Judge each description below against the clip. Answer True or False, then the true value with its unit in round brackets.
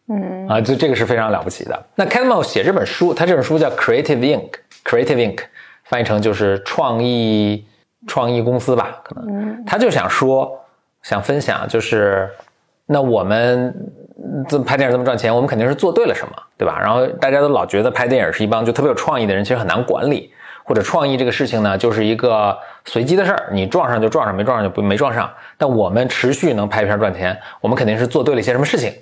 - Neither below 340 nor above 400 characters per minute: True (370 characters per minute)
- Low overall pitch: True (125 Hz)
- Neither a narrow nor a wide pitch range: False (6.4 semitones)